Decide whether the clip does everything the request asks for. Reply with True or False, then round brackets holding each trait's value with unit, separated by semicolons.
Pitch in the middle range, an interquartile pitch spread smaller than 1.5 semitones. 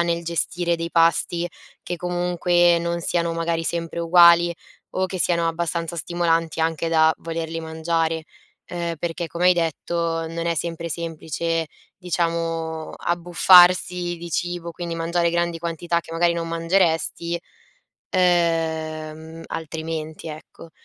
True (170 Hz; 0.9 semitones)